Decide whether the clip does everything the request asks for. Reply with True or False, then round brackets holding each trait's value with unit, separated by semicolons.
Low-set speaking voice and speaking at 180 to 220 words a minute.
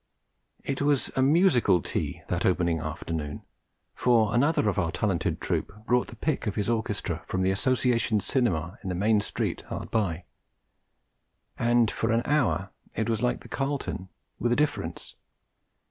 False (110 Hz; 160 wpm)